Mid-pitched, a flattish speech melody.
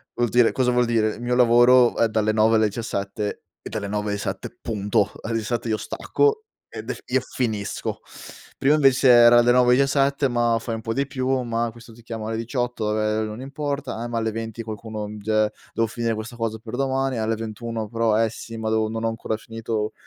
No: low, 115 Hz; narrow, 2.0 semitones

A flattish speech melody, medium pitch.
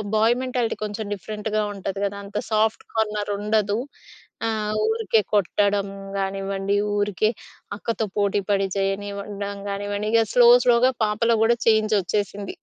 No: narrow, 1.6 semitones; high, 205 Hz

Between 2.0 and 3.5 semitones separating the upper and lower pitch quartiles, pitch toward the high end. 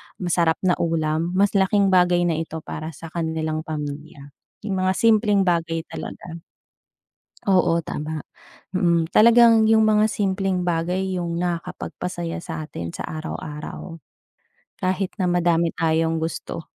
No: average, 2.8 semitones; medium, 170 Hz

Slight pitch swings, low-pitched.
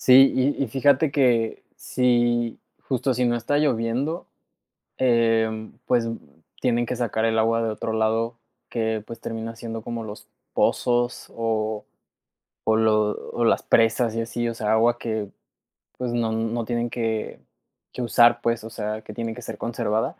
Yes: narrow, 1.4 semitones; low, 115 Hz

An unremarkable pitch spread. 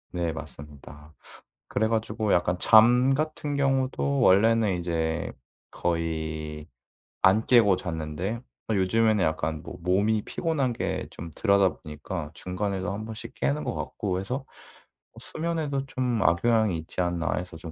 No: wide, 5.7 semitones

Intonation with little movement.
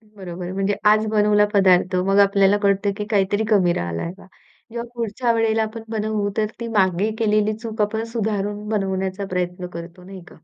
Yes: narrow, 2.3 semitones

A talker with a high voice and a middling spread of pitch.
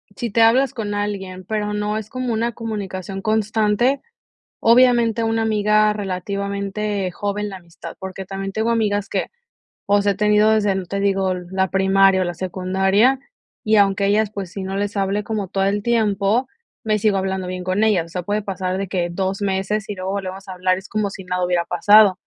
No: high, 200 Hz; narrow, 1.9 semitones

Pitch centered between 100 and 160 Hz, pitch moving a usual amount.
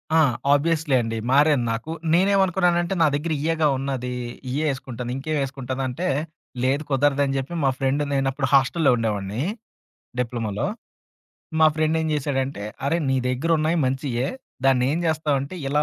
Yes: medium, 140 Hz; average, 3.3 semitones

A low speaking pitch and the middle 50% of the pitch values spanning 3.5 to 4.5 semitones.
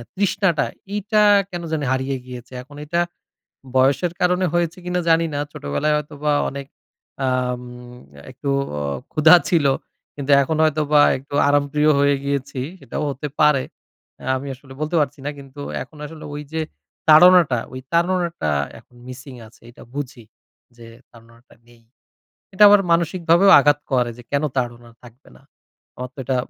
No: medium, 145 Hz; average, 4.1 semitones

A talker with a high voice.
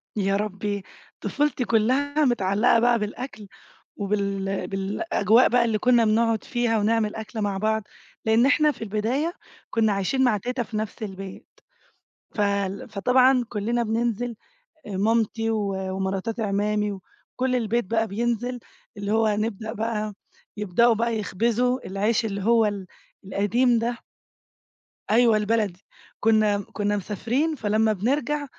Yes: high, 220 Hz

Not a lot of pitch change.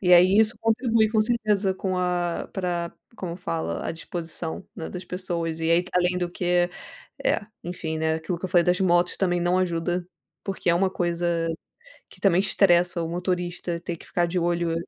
Yes: narrow, 1.5 semitones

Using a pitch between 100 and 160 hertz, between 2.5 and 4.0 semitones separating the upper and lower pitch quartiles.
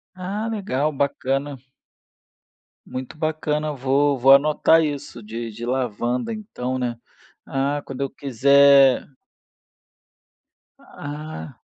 Yes: medium, 140 Hz; average, 2.8 semitones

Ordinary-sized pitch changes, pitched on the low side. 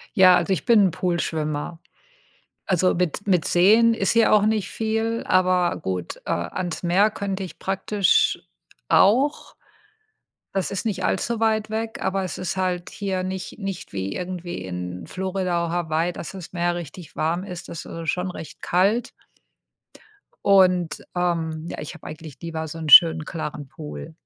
No: average, 3.1 semitones; medium, 180 Hz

